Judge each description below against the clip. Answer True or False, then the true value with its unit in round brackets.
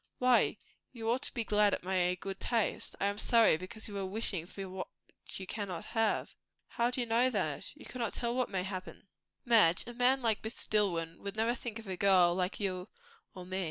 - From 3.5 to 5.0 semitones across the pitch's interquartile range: True (3.9 semitones)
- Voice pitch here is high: True (205 Hz)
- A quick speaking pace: True (215 wpm)